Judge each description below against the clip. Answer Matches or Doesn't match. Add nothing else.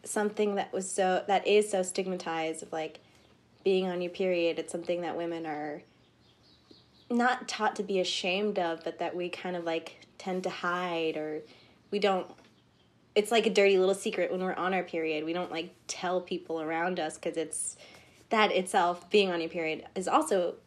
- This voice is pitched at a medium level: Matches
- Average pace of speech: Matches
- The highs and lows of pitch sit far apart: Doesn't match